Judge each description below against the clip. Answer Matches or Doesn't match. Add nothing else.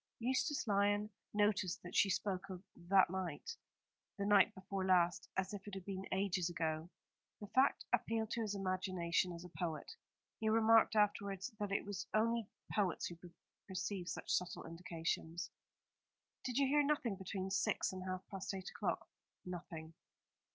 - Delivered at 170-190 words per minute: Doesn't match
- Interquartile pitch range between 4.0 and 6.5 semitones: Doesn't match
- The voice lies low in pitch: Doesn't match